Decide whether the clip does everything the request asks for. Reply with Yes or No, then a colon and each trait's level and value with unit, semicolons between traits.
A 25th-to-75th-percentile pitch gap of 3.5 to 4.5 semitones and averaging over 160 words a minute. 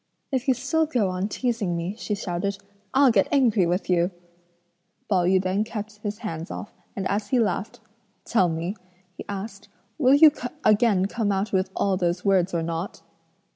Yes: average, 3.9 semitones; average, 175 wpm